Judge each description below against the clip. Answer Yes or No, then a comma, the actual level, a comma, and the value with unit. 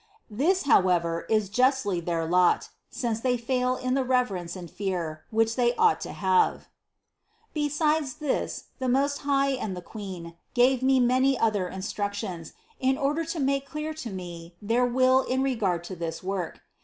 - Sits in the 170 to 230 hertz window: No, high, 240 Hz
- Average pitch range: No, wide, 6.4 semitones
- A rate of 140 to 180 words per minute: Yes, average, 165 wpm